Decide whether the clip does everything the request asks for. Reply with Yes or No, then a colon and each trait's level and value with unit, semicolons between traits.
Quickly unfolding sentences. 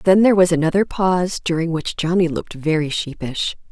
No: average, 180 wpm